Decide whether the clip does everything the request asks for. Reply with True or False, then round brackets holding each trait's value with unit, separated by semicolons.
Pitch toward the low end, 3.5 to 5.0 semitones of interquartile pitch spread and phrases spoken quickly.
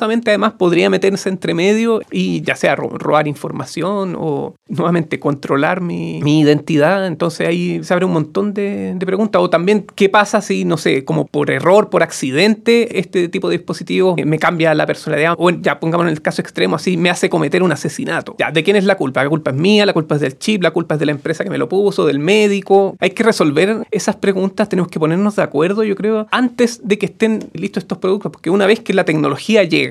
False (185 Hz; 3.8 semitones; 225 wpm)